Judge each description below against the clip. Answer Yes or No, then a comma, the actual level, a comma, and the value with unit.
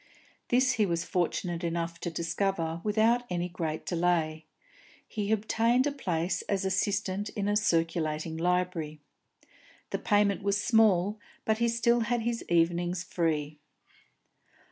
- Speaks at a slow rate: Yes, slow, 130 wpm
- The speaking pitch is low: No, medium, 180 Hz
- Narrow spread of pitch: No, average, 4.4 semitones